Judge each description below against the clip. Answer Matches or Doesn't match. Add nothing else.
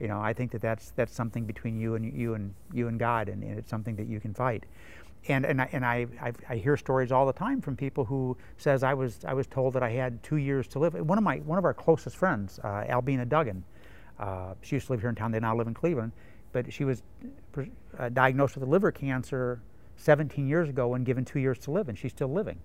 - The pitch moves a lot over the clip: Doesn't match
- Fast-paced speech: Matches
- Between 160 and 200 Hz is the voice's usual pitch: Doesn't match